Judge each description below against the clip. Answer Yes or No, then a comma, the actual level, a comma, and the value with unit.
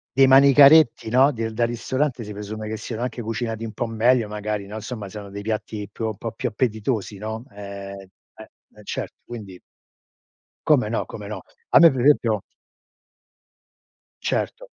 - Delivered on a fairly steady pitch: No, average, 3.0 semitones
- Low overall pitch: Yes, low, 110 Hz